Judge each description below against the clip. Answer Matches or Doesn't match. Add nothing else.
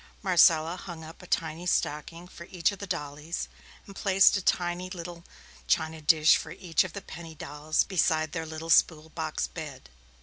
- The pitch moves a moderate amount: Doesn't match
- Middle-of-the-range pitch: Matches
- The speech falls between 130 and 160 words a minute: Doesn't match